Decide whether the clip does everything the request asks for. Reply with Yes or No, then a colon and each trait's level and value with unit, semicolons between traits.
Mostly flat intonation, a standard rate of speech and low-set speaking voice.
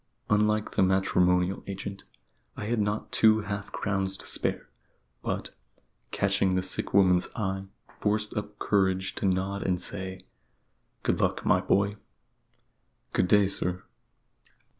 No: narrow, 1.8 semitones; slow, 130 wpm; low, 100 Hz